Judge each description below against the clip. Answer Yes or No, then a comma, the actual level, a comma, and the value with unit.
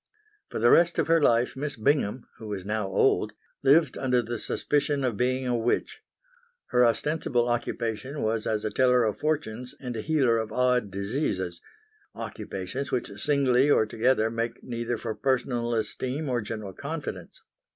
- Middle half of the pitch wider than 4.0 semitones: No, average, 3.4 semitones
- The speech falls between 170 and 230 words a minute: No, average, 160 wpm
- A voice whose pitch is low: Yes, low, 120 Hz